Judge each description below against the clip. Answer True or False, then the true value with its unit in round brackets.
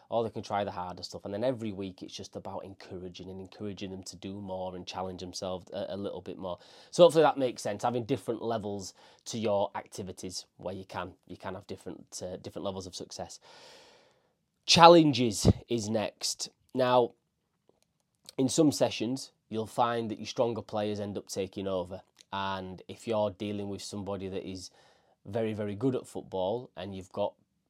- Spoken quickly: False (185 wpm)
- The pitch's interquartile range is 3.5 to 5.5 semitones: True (3.8 semitones)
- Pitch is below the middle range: True (100 Hz)